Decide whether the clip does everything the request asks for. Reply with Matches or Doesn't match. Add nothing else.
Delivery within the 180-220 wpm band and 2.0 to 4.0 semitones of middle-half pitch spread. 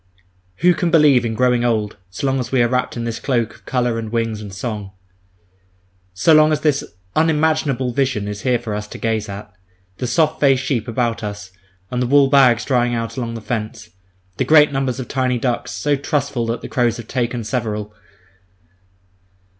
Matches